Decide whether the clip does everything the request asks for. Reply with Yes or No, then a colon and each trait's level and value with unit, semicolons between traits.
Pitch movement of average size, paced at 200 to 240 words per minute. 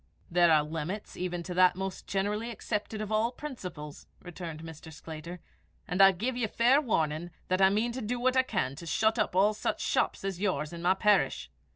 Yes: average, 4.5 semitones; fast, 205 wpm